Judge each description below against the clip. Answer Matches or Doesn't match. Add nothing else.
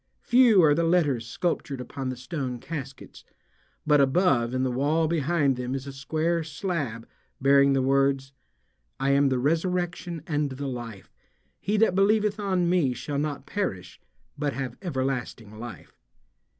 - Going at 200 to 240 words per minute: Doesn't match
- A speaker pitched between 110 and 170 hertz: Matches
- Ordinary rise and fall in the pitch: Matches